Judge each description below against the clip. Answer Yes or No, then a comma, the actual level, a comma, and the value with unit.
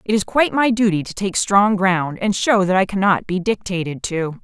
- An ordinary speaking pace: No, fast, 230 wpm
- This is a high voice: Yes, high, 195 Hz